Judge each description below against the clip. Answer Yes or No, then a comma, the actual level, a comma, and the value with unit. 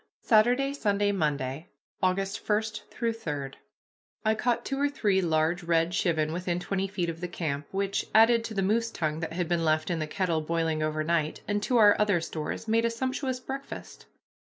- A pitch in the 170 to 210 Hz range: Yes, medium, 185 Hz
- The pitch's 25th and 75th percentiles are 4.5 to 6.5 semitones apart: Yes, average, 5.3 semitones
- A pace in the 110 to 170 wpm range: No, average, 190 wpm